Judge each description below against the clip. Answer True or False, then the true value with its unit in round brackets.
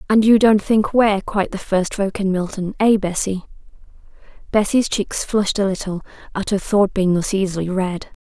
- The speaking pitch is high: True (200 Hz)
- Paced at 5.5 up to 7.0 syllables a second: False (5.2 syllables/s)